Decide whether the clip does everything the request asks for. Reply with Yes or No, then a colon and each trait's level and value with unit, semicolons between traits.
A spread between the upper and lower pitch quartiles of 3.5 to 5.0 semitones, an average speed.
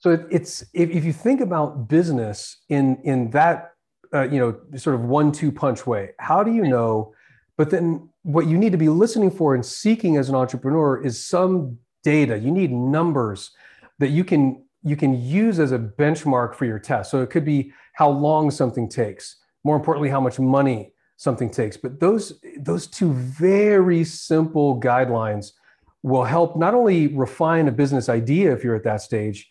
Yes: average, 4.7 semitones; average, 185 wpm